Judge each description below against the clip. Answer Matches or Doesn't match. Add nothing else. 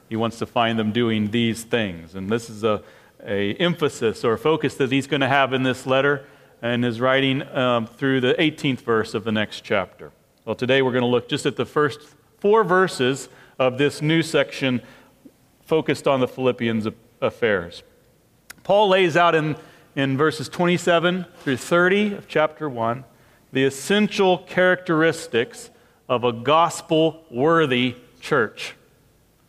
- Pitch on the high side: Doesn't match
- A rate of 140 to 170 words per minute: Matches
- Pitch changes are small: Doesn't match